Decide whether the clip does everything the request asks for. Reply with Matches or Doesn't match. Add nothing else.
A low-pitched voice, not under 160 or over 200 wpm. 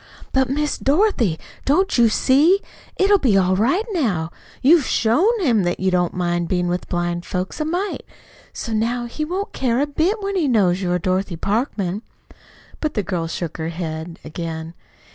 Doesn't match